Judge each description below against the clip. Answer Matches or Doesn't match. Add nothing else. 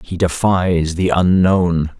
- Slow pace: Matches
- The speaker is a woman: Doesn't match